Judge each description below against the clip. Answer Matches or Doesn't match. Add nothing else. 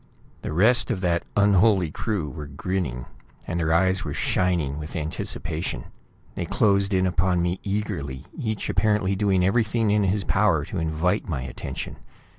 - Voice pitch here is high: Doesn't match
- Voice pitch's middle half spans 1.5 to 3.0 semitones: Doesn't match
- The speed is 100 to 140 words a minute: Doesn't match